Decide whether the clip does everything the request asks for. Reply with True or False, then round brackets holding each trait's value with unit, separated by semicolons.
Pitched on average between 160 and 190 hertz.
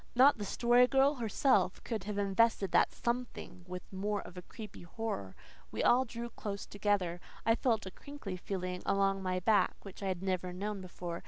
False (200 Hz)